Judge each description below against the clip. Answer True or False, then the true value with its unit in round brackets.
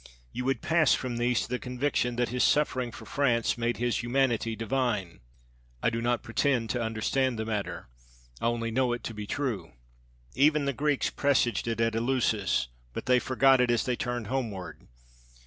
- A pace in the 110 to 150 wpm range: False (180 wpm)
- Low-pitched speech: True (120 Hz)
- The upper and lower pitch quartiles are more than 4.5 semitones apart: False (2.5 semitones)